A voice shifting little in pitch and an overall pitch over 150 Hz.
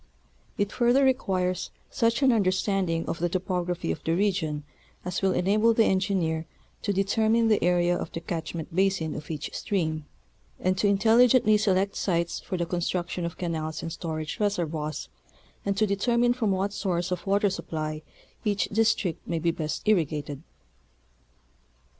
No: average, 3.7 semitones; medium, 185 Hz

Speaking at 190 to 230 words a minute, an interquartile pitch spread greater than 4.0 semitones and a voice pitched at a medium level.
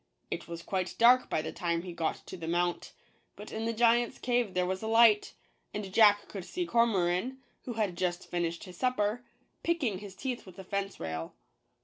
No: average, 200 wpm; average, 4.7 semitones; high, 200 Hz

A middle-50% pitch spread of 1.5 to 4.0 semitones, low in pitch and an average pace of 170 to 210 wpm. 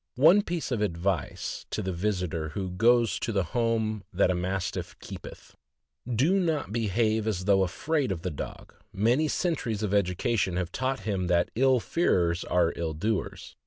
No: average, 4.8 semitones; low, 105 Hz; average, 180 wpm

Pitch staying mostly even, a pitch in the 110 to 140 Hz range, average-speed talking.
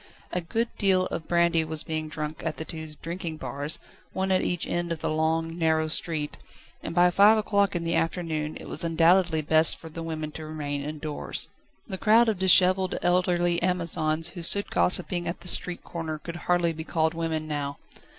No: narrow, 2.2 semitones; medium, 165 Hz; average, 190 wpm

